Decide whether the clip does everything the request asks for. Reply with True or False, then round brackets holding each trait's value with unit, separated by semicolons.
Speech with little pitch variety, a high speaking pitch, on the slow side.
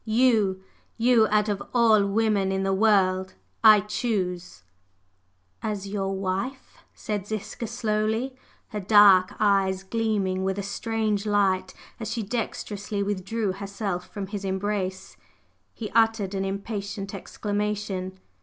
True (2.1 semitones; 205 Hz; 125 wpm)